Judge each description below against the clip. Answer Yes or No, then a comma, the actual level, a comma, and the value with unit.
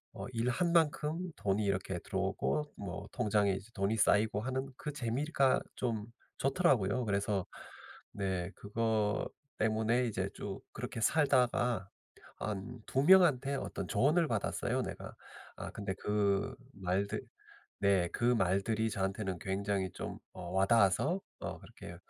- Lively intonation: No, average, 4.5 semitones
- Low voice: Yes, low, 110 Hz